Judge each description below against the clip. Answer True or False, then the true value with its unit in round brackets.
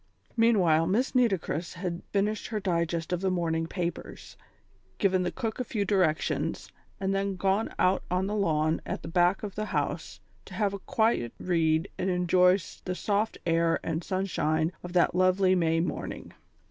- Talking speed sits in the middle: True (170 wpm)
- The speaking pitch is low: False (185 Hz)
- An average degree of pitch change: True (3.0 semitones)